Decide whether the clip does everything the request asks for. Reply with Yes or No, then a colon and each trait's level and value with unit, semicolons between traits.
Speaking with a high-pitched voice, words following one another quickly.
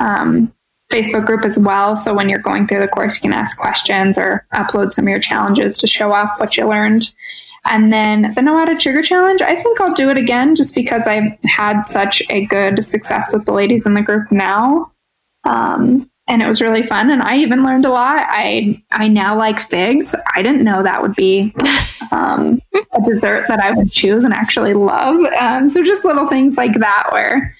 Yes: high, 225 Hz; fast, 215 wpm